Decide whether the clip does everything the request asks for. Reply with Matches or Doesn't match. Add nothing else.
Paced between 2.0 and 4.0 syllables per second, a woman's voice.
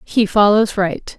Matches